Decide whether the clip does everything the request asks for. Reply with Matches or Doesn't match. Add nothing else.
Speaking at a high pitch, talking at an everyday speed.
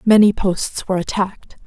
Matches